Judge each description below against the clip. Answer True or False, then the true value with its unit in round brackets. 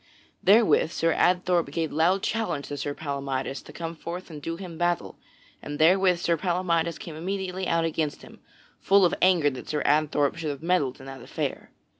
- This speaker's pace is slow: False (185 wpm)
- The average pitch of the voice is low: False (165 Hz)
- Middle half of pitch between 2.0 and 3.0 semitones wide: False (3.5 semitones)